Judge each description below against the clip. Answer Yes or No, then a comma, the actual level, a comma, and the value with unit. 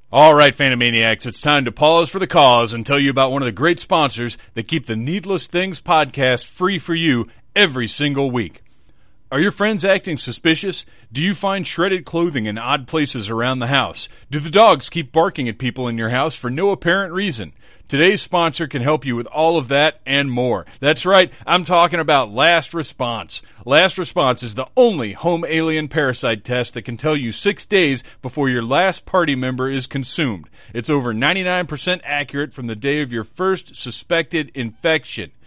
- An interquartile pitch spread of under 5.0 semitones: No, wide, 5.4 semitones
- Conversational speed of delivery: Yes, average, 190 wpm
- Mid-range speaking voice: Yes, medium, 145 Hz